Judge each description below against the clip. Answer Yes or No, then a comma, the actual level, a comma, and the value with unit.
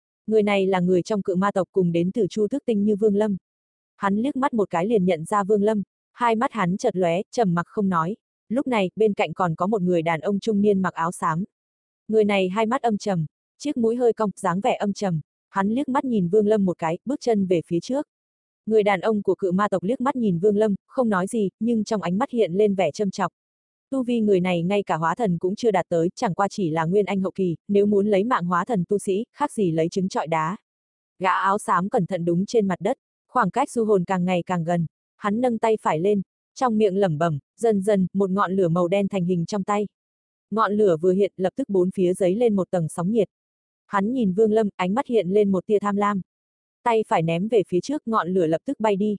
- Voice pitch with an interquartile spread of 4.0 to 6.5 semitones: No, average, 3.1 semitones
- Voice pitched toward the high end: Yes, high, 200 Hz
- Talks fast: Yes, fast, 255 wpm